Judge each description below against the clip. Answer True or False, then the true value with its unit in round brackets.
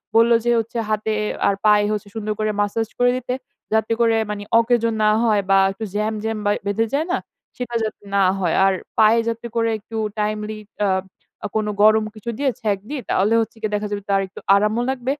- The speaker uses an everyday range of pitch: False (1.7 semitones)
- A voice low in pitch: False (215 Hz)